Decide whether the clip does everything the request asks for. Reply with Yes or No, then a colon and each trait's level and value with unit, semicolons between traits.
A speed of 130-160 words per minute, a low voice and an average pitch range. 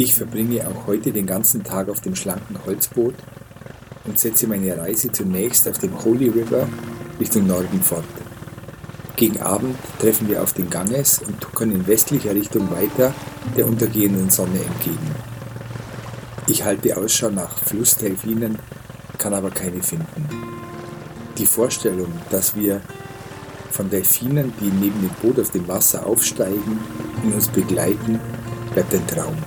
Yes: average, 140 wpm; low, 115 Hz; average, 3.9 semitones